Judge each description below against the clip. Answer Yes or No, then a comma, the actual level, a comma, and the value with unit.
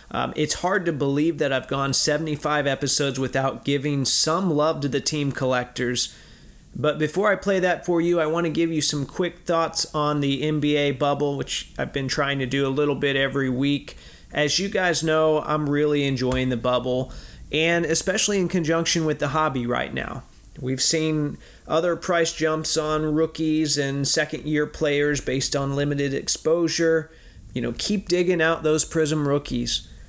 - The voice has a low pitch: No, medium, 150 Hz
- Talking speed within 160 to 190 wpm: Yes, average, 180 wpm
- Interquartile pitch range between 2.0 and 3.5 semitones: Yes, average, 2.8 semitones